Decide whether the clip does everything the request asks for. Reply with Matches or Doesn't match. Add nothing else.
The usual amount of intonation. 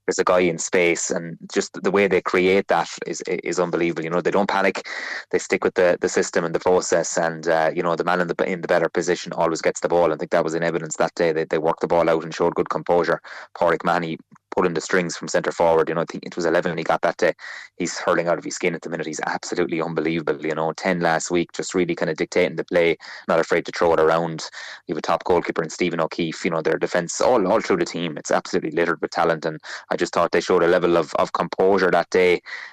Doesn't match